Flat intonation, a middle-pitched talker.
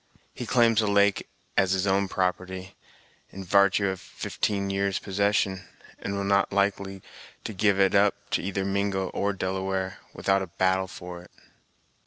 No: narrow, 1.0 semitones; very low, 95 Hz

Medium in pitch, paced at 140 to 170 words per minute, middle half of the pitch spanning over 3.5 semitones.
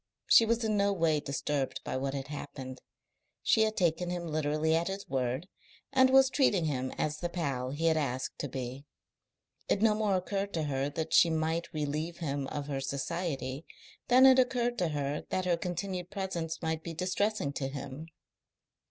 No: medium, 160 Hz; average, 185 wpm; average, 5.0 semitones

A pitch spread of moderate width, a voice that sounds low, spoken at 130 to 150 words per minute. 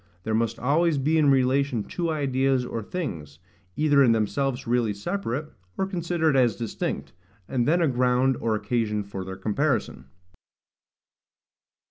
Yes: average, 4.9 semitones; low, 130 Hz; average, 140 wpm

